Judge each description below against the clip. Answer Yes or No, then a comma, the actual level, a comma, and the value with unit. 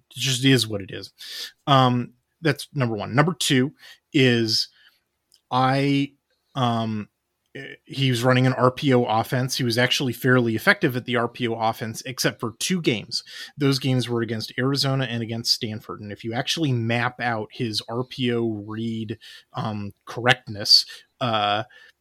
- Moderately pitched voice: No, low, 125 Hz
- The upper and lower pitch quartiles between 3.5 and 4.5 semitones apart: No, narrow, 2.5 semitones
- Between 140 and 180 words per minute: Yes, average, 145 wpm